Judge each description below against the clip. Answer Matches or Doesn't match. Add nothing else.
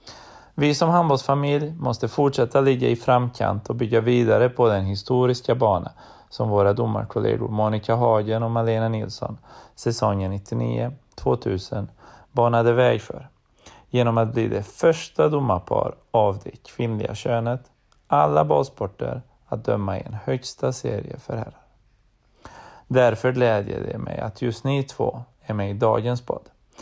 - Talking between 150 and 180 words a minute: Doesn't match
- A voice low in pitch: Matches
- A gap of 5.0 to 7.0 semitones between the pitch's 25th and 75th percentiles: Doesn't match